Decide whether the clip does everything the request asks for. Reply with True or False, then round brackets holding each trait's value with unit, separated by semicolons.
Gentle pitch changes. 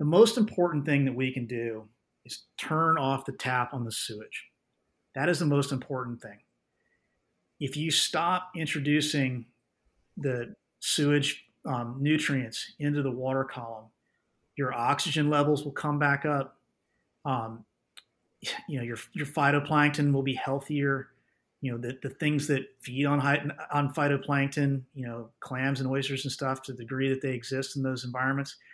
True (2.1 semitones)